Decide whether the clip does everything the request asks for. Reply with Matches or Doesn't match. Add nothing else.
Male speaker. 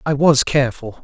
Matches